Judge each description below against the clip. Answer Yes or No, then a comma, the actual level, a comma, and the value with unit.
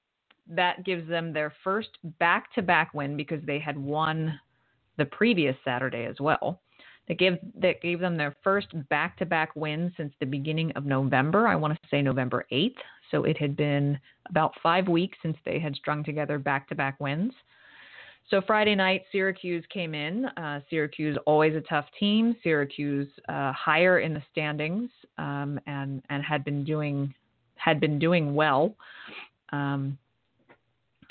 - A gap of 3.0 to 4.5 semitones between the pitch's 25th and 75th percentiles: Yes, average, 3.5 semitones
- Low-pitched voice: No, medium, 155 Hz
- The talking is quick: No, average, 165 wpm